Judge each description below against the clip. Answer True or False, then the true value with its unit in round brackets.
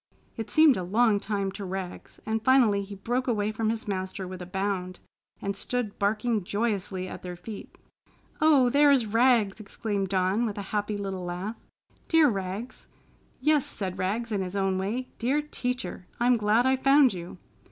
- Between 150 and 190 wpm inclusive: True (175 wpm)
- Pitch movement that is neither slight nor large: True (4.0 semitones)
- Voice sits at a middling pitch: False (210 Hz)